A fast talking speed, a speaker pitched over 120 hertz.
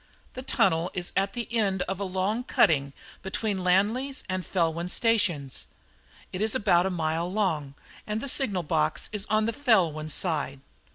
No: average, 165 wpm; high, 190 Hz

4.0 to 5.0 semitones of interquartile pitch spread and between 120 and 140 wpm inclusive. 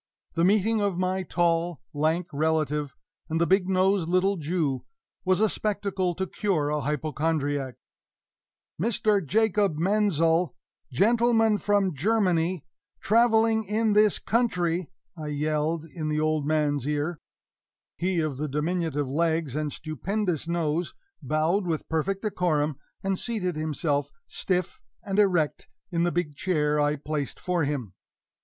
Yes: average, 4.3 semitones; slow, 135 wpm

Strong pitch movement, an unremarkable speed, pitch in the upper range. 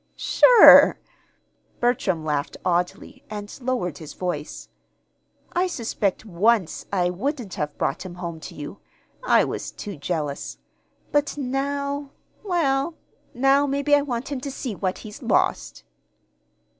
No: wide, 8.0 semitones; slow, 130 wpm; high, 220 Hz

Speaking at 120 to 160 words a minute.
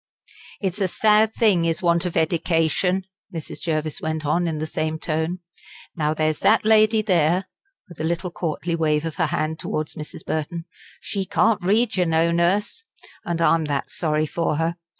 No: average, 175 wpm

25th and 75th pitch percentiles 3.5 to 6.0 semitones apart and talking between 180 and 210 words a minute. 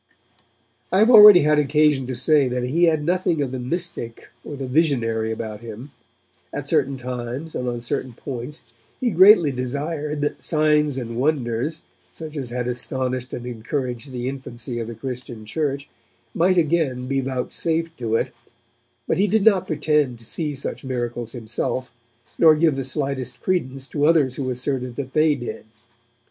No: average, 3.9 semitones; average, 165 wpm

